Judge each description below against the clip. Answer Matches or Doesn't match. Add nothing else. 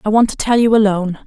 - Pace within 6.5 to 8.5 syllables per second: Matches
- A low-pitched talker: Doesn't match